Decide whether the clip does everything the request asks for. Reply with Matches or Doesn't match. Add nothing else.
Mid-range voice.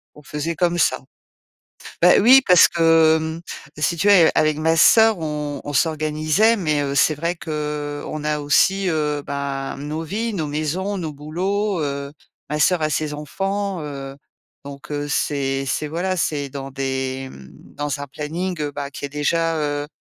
Matches